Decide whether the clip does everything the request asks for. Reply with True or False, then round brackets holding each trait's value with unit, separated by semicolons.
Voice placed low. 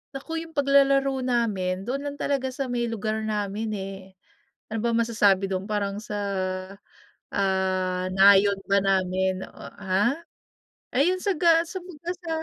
False (220 Hz)